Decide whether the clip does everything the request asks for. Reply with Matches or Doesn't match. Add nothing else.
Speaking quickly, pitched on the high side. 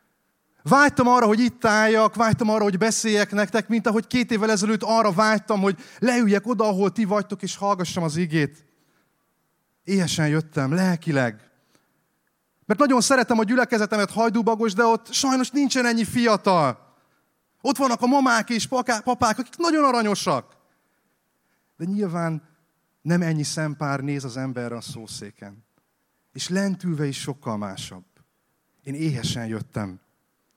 Doesn't match